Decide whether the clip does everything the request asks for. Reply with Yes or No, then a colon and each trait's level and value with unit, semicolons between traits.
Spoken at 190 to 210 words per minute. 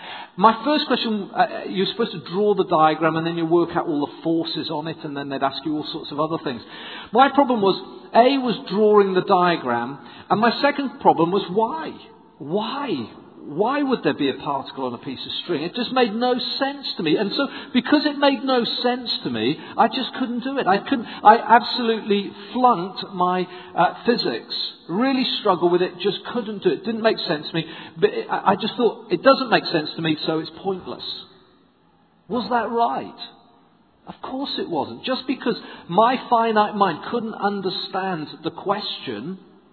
Yes: average, 195 wpm